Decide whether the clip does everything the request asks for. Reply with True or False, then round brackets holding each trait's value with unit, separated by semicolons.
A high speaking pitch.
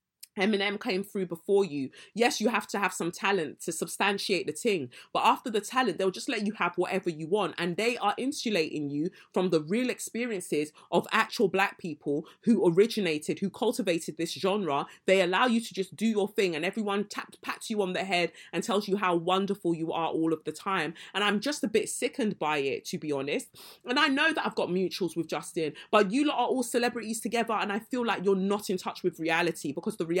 True (195 Hz)